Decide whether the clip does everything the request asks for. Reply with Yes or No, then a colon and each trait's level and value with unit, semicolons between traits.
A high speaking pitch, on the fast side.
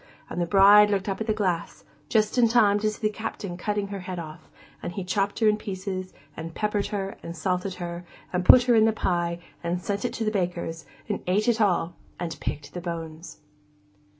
Yes: high, 195 Hz; fast, 215 wpm